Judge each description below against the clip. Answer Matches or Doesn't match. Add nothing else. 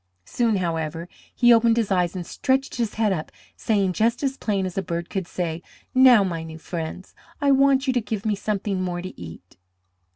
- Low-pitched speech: Doesn't match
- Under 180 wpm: Doesn't match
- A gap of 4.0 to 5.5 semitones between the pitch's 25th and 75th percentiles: Matches